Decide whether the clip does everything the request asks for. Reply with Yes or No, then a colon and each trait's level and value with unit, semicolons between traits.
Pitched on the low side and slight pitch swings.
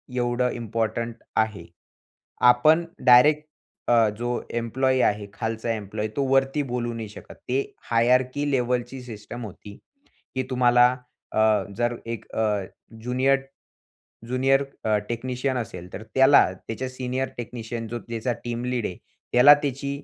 Yes: low, 120 Hz; narrow, 2.3 semitones